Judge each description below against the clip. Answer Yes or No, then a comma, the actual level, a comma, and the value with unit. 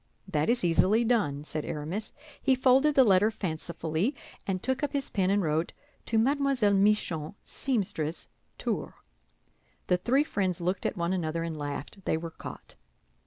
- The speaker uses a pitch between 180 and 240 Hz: Yes, high, 190 Hz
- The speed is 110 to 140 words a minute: No, average, 160 wpm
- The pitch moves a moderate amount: No, wide, 6.4 semitones